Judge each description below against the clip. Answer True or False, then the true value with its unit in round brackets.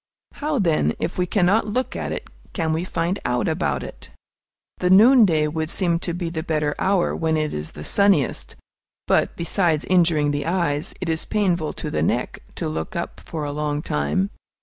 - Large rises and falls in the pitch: False (3.6 semitones)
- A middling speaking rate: True (190 wpm)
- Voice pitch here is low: False (165 Hz)